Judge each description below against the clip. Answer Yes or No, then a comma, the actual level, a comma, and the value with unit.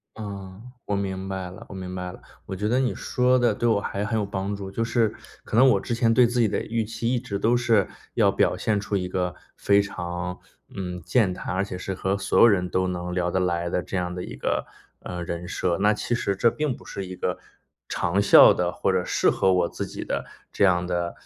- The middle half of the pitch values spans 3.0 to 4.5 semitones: Yes, average, 3.6 semitones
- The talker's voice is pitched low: Yes, low, 100 Hz